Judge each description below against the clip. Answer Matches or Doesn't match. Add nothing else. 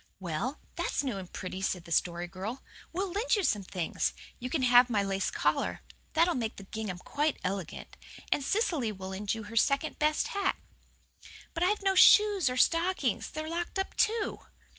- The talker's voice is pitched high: Matches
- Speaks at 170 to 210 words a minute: Matches